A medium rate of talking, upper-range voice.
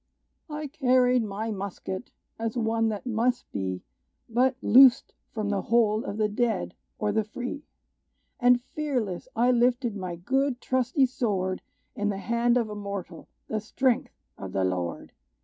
Yes: average, 150 wpm; high, 230 Hz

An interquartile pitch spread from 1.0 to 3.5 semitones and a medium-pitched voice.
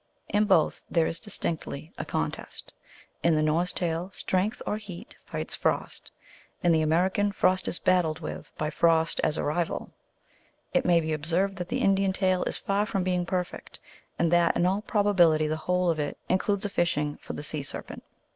Yes: average, 3.0 semitones; medium, 175 Hz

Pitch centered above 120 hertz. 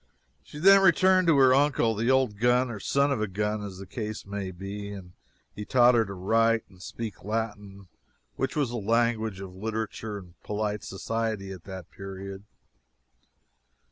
No: low, 110 Hz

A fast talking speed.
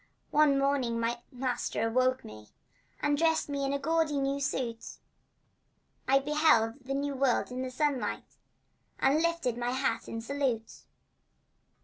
No: slow, 135 wpm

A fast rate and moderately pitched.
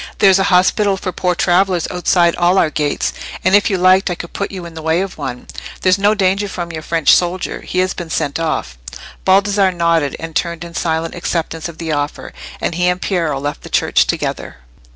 Yes: fast, 215 wpm; medium, 175 Hz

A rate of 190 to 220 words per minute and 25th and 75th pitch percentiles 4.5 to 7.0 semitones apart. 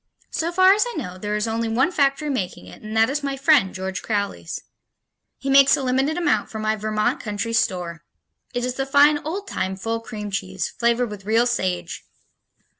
Yes: average, 195 wpm; average, 5.1 semitones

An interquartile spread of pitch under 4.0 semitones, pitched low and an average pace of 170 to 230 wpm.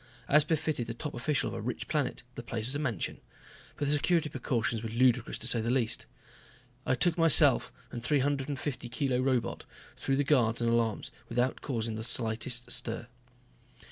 Yes: average, 3.6 semitones; low, 125 Hz; average, 190 wpm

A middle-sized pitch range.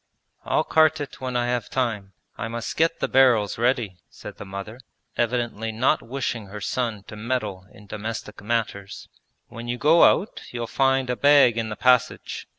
Yes: average, 3.3 semitones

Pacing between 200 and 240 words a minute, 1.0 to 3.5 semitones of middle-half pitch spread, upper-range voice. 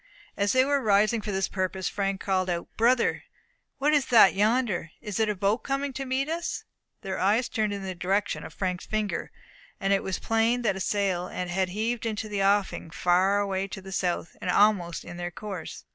Yes: fast, 205 wpm; average, 3.1 semitones; high, 200 Hz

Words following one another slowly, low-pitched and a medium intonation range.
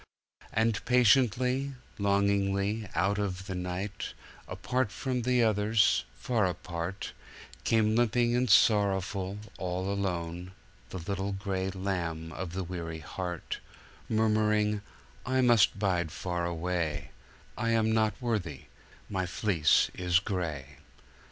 Yes: slow, 115 wpm; low, 100 Hz; average, 3.6 semitones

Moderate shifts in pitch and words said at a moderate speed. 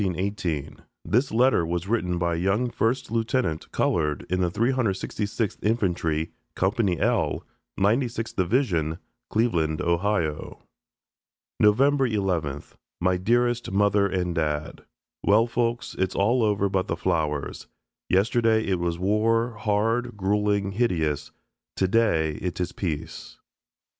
No: average, 4.9 semitones; slow, 125 wpm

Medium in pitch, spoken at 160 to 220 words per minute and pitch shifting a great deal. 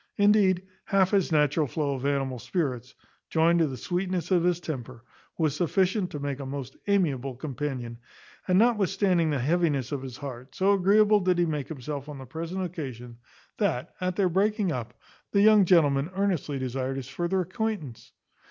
Yes: medium, 160 Hz; average, 170 wpm; wide, 5.7 semitones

